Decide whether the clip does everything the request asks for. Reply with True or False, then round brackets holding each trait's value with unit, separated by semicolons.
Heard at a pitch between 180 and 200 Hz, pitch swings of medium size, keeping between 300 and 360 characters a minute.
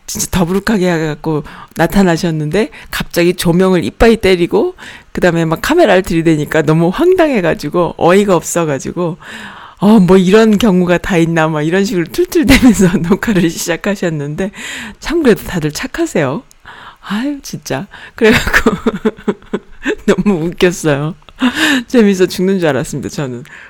True (185 Hz; 4.7 semitones; 315 characters per minute)